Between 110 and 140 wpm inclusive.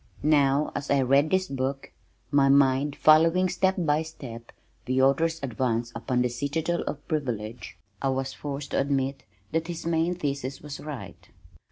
No: average, 160 wpm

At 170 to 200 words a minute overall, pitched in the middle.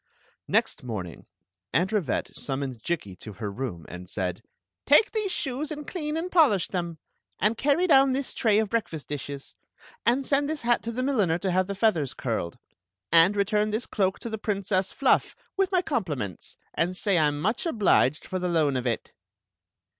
No: average, 185 wpm; high, 195 Hz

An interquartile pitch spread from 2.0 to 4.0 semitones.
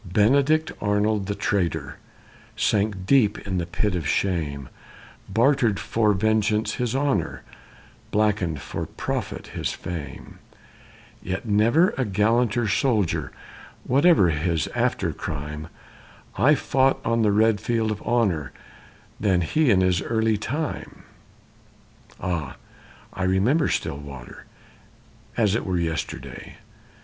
No: average, 4.7 semitones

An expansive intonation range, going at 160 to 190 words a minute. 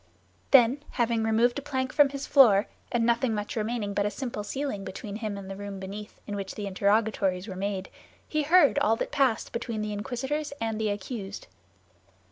No: average, 4.2 semitones; average, 185 wpm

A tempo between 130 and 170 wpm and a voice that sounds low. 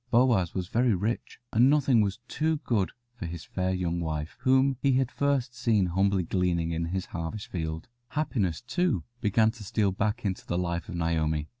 No: average, 185 wpm; very low, 95 Hz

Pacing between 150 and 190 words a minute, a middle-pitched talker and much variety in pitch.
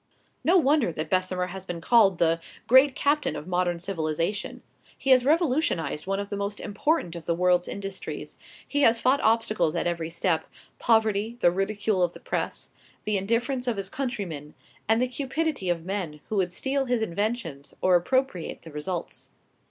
No: average, 175 wpm; high, 200 Hz; wide, 5.8 semitones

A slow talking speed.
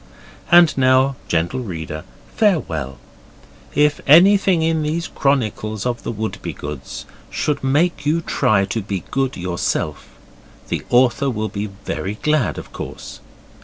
Yes: slow, 130 wpm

